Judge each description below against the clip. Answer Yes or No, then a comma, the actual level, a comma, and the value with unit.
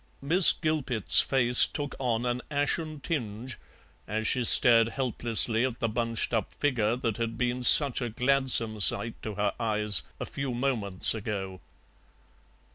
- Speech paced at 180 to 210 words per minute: No, average, 145 wpm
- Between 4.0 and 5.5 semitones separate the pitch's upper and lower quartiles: No, average, 3.3 semitones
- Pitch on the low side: Yes, low, 120 Hz